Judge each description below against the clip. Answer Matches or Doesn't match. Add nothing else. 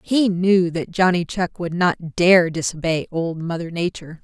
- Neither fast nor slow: Matches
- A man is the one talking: Doesn't match